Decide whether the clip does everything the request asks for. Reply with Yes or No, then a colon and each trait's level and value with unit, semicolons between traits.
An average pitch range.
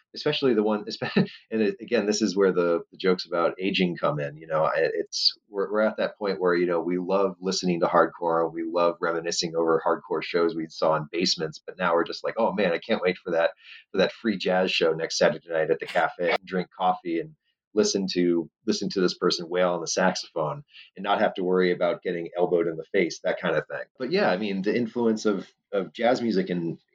Yes: average, 3.6 semitones